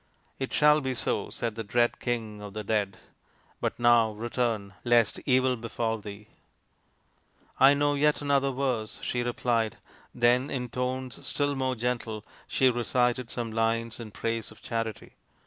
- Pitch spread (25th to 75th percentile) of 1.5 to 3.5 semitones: Yes, narrow, 2.4 semitones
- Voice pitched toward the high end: No, low, 120 Hz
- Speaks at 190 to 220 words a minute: No, average, 165 wpm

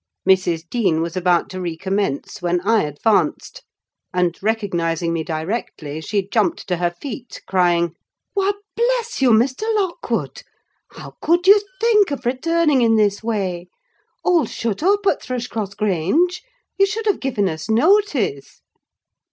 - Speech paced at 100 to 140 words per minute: Yes, slow, 135 wpm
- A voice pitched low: No, high, 215 Hz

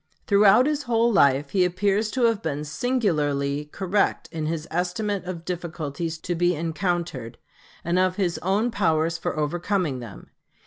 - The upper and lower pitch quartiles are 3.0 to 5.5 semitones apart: Yes, average, 4.5 semitones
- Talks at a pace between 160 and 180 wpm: No, average, 150 wpm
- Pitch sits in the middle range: Yes, medium, 175 Hz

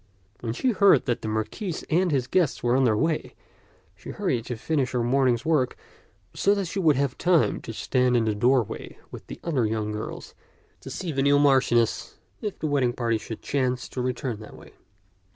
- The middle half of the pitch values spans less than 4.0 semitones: No, average, 4.7 semitones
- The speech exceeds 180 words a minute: Yes, average, 200 wpm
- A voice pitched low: Yes, low, 130 Hz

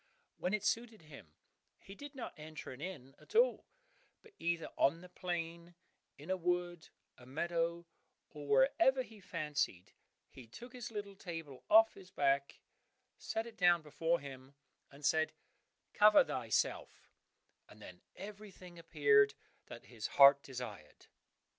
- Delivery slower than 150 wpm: Yes, average, 140 wpm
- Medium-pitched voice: Yes, medium, 170 Hz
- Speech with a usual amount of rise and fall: No, wide, 5.9 semitones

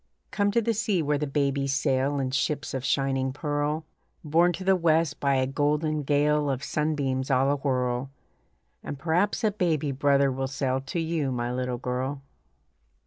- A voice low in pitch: No, medium, 145 Hz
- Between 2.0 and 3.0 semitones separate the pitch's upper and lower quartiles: Yes, average, 2.7 semitones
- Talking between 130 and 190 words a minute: Yes, average, 175 wpm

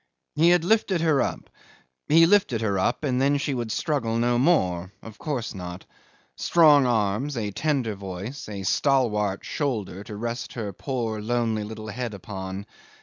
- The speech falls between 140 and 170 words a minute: Yes, average, 160 wpm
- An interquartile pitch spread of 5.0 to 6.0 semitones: Yes, wide, 5.5 semitones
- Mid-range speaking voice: No, low, 115 Hz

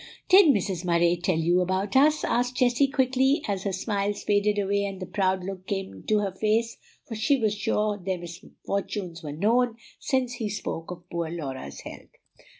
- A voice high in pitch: Yes, high, 200 Hz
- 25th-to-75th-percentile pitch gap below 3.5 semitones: No, average, 4.3 semitones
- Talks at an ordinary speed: Yes, average, 180 wpm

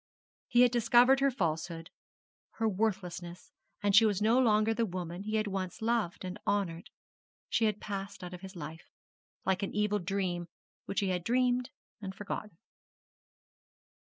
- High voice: Yes, high, 200 Hz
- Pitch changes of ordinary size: Yes, average, 3.7 semitones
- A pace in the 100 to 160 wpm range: Yes, average, 155 wpm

